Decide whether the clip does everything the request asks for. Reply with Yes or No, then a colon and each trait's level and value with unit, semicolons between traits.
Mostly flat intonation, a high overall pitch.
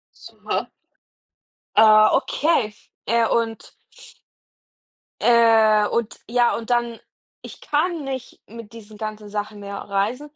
Yes: narrow, 2.2 semitones; high, 230 Hz